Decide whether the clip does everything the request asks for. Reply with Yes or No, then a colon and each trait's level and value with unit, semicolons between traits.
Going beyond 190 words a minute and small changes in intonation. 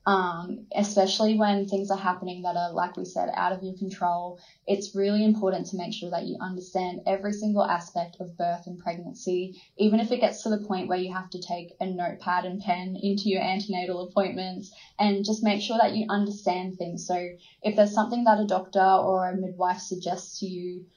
Yes: fast, 205 wpm; narrow, 2.1 semitones